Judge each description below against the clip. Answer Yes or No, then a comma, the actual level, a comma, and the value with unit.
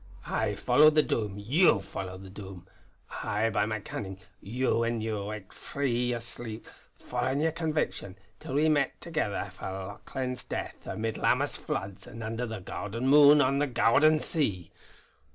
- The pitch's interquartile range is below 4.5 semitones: No, wide, 5.5 semitones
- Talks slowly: No, average, 160 wpm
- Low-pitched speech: Yes, low, 115 Hz